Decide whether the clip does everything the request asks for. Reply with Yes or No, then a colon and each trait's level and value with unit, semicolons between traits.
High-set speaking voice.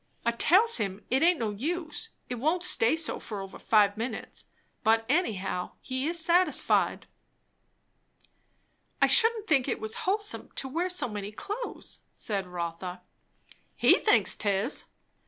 Yes: very high, 255 Hz